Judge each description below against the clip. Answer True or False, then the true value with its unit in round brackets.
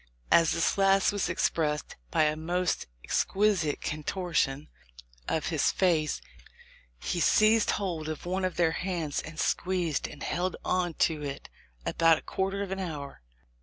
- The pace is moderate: True (155 wpm)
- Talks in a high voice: False (170 Hz)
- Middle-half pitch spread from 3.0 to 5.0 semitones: True (3.5 semitones)